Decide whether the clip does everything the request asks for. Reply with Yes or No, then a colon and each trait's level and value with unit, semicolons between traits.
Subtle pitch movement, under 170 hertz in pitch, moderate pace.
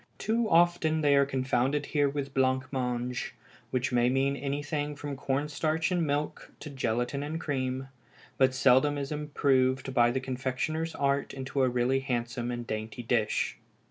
Yes: narrow, 2.3 semitones; low, 135 Hz; average, 160 wpm